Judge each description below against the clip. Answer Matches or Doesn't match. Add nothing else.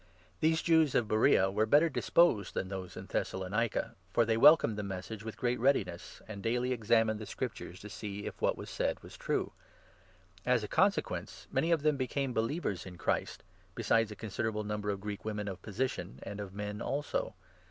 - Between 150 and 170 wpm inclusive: Doesn't match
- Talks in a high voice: Doesn't match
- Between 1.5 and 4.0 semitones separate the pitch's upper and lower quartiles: Matches